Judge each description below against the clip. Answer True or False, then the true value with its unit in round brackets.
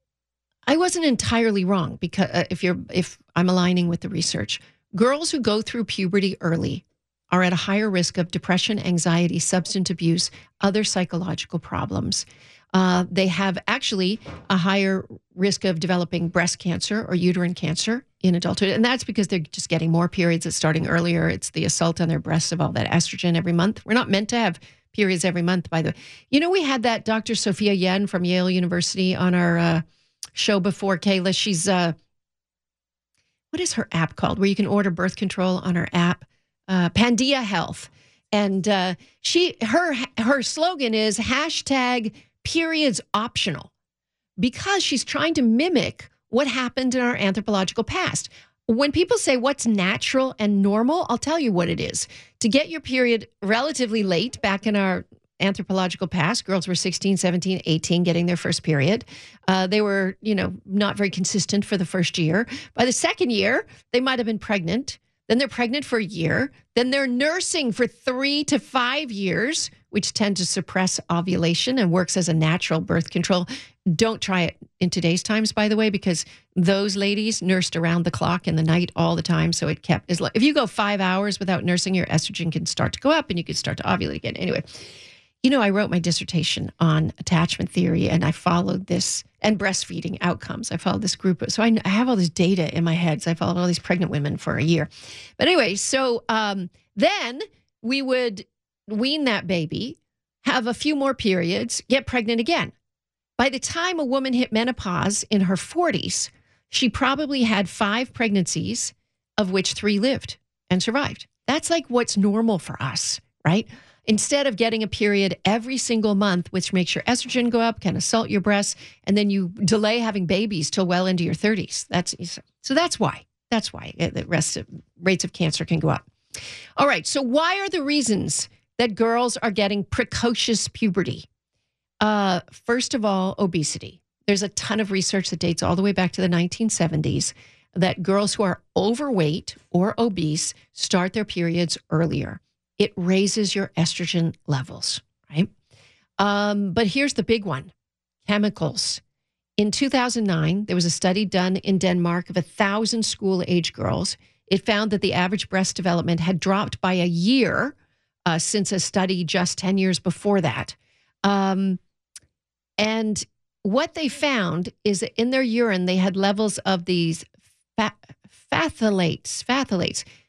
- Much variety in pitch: False (4.5 semitones)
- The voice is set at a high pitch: True (195 Hz)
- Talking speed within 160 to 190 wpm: True (180 wpm)